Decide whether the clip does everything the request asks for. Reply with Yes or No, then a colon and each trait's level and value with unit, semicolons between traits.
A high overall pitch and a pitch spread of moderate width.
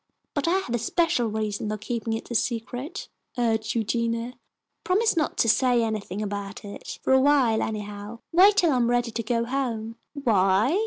Yes: high, 230 Hz; average, 3.4 semitones